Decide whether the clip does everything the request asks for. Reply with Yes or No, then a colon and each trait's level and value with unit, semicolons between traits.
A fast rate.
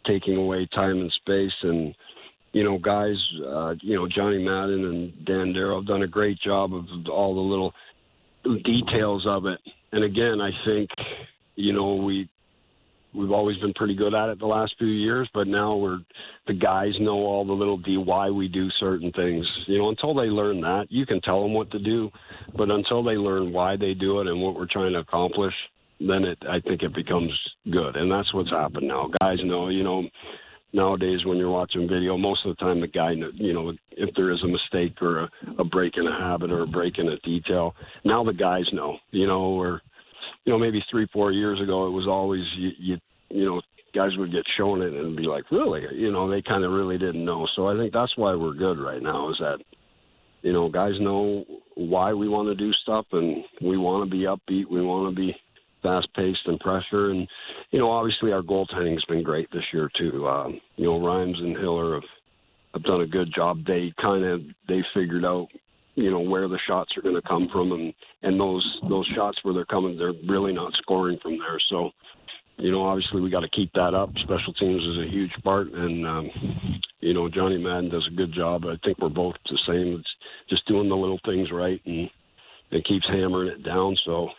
Yes: fast, 220 wpm